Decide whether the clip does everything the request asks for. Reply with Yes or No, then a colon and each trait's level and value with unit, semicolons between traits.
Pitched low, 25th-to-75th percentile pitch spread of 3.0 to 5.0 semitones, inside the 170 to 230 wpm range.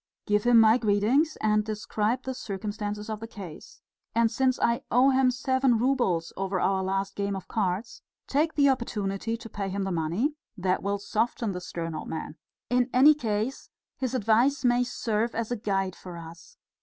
No: high, 215 Hz; average, 4.1 semitones; average, 180 wpm